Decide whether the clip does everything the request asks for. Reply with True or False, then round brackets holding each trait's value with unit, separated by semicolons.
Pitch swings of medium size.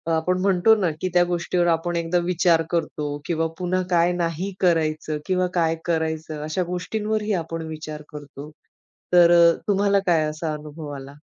False (2.3 semitones)